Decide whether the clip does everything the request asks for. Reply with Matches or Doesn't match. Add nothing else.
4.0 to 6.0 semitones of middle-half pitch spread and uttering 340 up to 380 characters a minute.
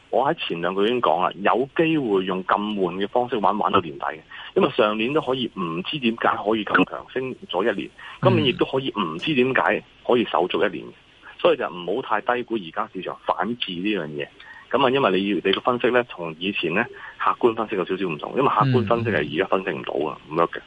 Matches